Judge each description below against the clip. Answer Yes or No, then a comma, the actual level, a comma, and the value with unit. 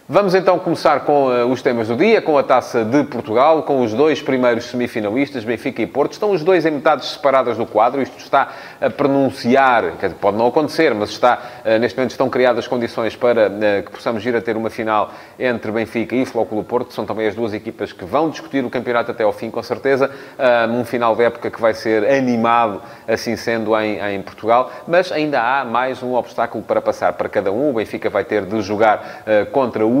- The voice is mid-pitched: No, low, 120 Hz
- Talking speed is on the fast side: Yes, fast, 220 wpm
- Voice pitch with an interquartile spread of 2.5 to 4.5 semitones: Yes, average, 3.5 semitones